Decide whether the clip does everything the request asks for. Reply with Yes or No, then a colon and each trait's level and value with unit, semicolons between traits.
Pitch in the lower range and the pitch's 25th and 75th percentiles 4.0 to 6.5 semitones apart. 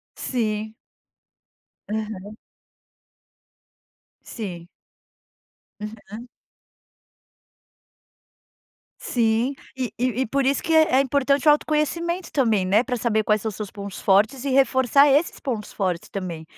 No: high, 230 Hz; average, 4.6 semitones